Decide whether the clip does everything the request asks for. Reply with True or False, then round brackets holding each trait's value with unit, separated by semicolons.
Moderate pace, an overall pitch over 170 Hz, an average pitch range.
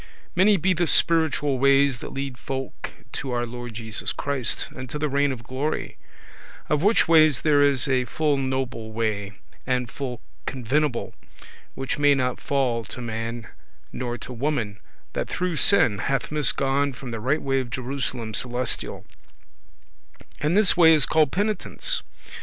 False (155 wpm; 135 Hz; 3.6 semitones)